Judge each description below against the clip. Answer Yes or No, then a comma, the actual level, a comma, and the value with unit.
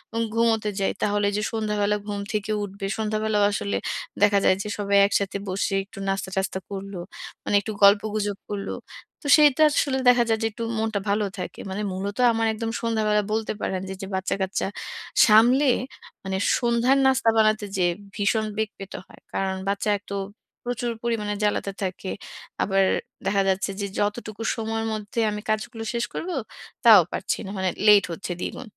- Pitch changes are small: Yes, narrow, 2.0 semitones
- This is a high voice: Yes, high, 210 Hz